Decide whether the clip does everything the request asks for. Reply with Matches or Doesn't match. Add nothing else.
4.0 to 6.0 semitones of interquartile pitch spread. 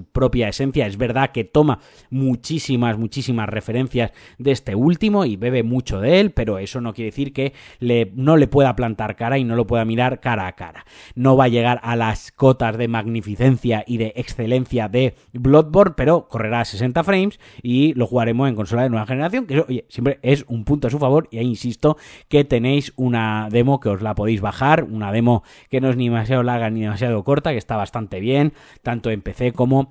Doesn't match